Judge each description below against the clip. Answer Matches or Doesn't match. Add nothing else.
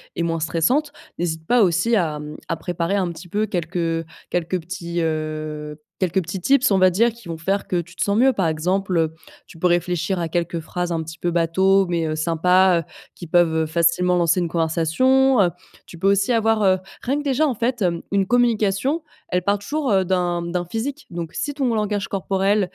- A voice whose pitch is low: Doesn't match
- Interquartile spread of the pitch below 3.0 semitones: Doesn't match